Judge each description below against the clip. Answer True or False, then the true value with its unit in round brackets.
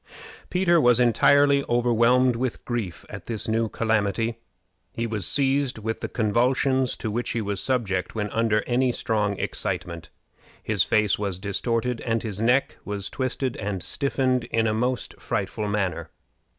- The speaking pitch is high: False (115 Hz)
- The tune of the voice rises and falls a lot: False (3.3 semitones)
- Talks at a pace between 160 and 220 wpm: False (150 wpm)